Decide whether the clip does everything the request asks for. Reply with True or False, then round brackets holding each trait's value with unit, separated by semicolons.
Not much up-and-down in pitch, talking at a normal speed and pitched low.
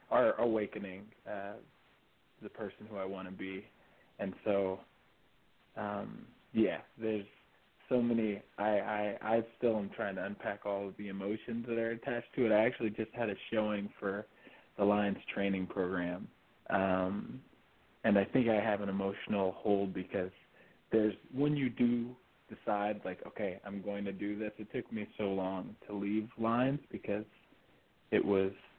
True (2.1 semitones; 165 wpm; 105 Hz)